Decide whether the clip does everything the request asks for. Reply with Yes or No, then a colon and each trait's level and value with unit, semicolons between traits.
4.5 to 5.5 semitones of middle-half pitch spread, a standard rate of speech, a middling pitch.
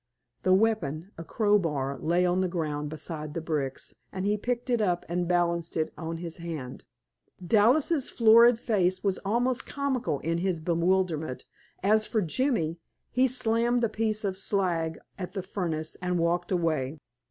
Yes: average, 4.9 semitones; average, 160 wpm; medium, 180 Hz